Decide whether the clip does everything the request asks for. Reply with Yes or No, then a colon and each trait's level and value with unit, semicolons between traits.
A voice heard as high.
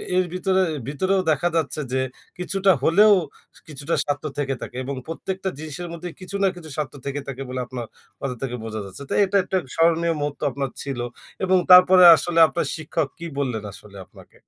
No: medium, 160 Hz